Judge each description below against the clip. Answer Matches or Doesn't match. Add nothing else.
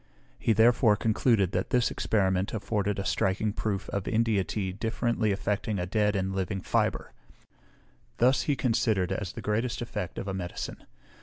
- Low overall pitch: Matches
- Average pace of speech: Matches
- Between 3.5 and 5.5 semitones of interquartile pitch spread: Doesn't match